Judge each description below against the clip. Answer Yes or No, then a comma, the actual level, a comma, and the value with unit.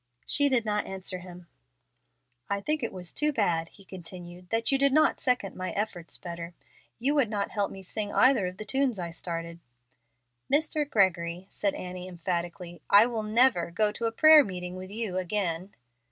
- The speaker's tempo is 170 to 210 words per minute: Yes, average, 180 wpm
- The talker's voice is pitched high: Yes, high, 195 Hz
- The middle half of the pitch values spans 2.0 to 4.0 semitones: No, average, 4.5 semitones